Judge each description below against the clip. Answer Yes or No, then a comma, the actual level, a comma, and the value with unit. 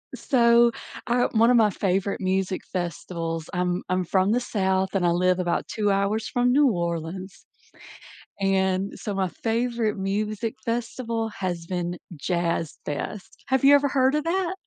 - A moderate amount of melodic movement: Yes, average, 4.5 semitones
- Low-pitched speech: No, high, 195 Hz